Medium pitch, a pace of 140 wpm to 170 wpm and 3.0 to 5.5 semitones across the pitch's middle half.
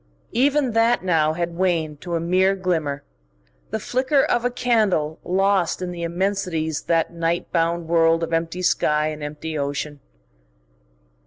Yes: medium, 170 Hz; average, 155 wpm; average, 3.5 semitones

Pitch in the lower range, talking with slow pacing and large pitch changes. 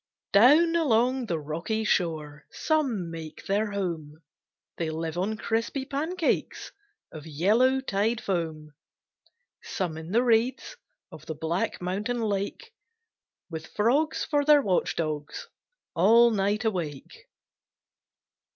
No: high, 200 Hz; slow, 115 wpm; wide, 7.0 semitones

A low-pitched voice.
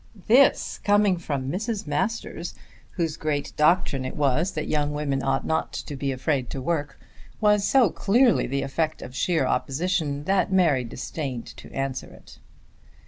No: medium, 150 Hz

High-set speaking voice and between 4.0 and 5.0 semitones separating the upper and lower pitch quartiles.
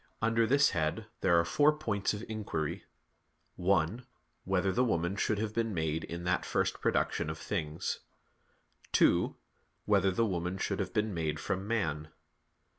No: very low, 95 Hz; average, 4.6 semitones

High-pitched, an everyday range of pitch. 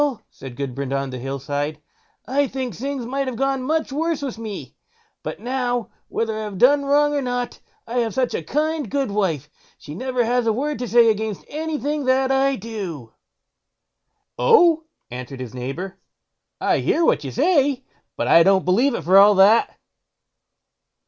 No: high, 240 Hz; wide, 6.8 semitones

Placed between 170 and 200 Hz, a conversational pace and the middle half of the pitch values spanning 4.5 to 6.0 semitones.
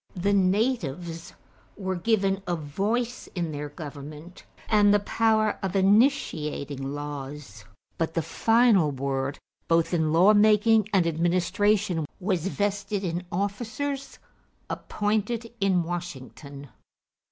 No: medium, 185 Hz; slow, 110 wpm; average, 5.1 semitones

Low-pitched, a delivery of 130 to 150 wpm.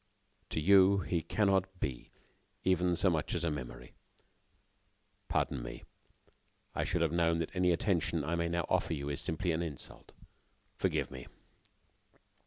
Yes: very low, 85 Hz; average, 145 wpm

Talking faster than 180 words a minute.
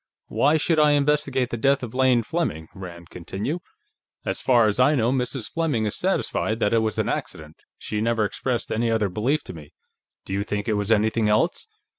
Yes: average, 200 wpm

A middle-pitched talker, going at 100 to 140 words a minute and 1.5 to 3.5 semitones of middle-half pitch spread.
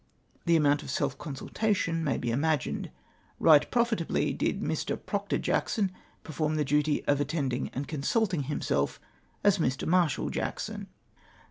Yes: medium, 150 Hz; slow, 135 wpm; average, 3.1 semitones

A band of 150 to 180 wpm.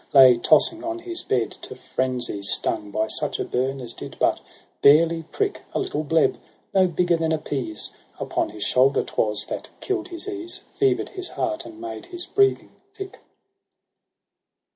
Yes: average, 165 wpm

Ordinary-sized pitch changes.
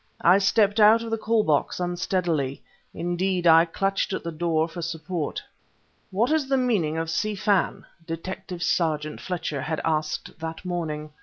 Yes: average, 3.4 semitones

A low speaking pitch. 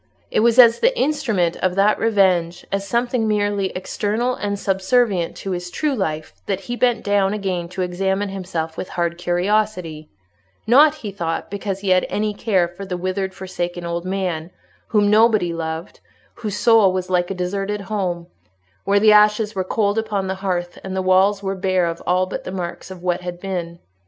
No: high, 190 Hz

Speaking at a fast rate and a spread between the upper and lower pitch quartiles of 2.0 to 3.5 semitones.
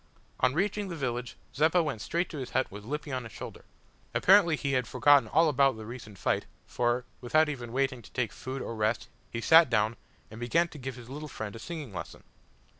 No: fast, 215 wpm; average, 4.5 semitones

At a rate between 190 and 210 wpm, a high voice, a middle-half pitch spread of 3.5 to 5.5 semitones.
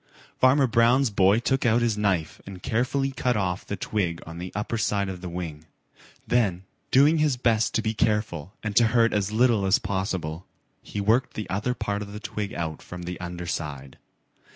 No: average, 195 wpm; low, 105 Hz; average, 4.6 semitones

